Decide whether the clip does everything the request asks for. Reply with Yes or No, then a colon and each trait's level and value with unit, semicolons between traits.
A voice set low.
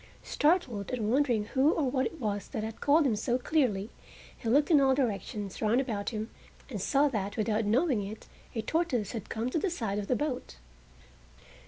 No: high, 240 Hz